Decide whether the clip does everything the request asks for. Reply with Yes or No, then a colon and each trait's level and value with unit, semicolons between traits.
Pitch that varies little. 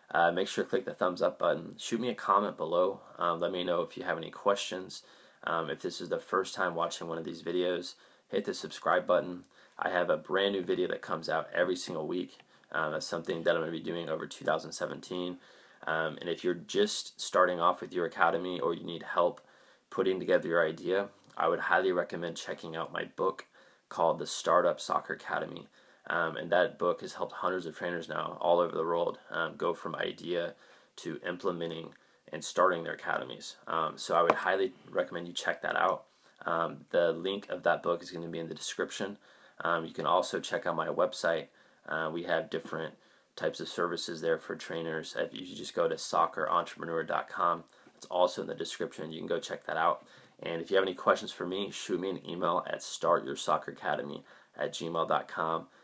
Yes: narrow, 2.2 semitones